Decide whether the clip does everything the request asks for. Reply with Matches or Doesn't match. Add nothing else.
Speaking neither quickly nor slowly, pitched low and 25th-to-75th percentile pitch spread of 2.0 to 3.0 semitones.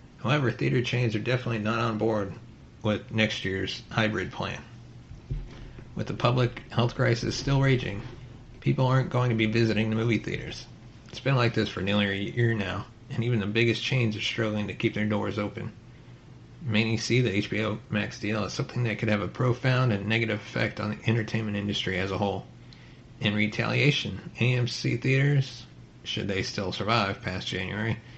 Matches